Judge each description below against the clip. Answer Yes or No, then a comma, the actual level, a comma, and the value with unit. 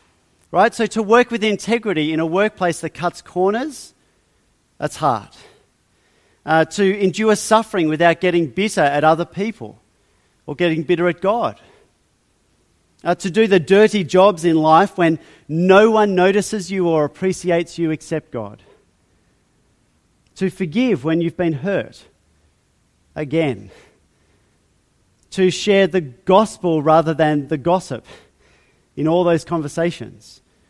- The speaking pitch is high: No, medium, 175 Hz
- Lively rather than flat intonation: No, average, 3.6 semitones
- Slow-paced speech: Yes, slow, 130 wpm